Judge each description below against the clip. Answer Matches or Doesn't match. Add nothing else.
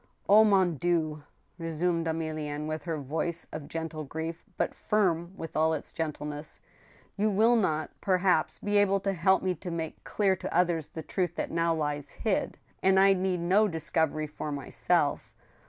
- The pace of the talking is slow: Doesn't match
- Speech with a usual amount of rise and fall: Matches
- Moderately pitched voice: Matches